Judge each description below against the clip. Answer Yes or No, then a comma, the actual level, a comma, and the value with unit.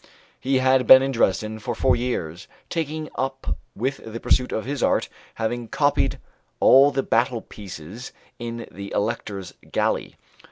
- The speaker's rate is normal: Yes, average, 150 wpm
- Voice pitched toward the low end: Yes, low, 120 Hz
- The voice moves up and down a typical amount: Yes, average, 3.5 semitones